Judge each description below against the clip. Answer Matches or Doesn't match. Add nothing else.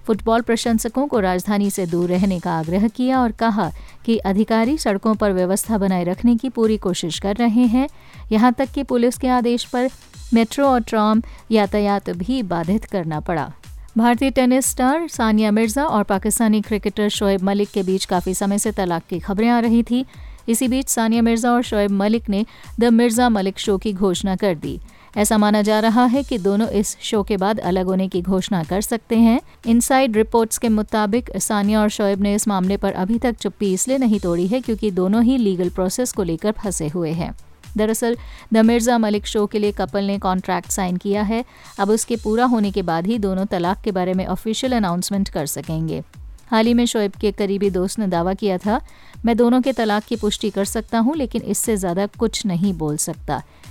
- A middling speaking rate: Doesn't match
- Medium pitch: Doesn't match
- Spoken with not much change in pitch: Doesn't match